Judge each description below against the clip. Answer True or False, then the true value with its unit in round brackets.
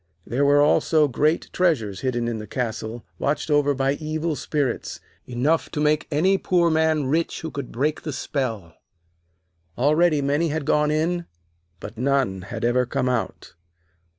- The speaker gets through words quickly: False (155 wpm)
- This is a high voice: False (145 Hz)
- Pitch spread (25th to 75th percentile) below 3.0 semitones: False (3.8 semitones)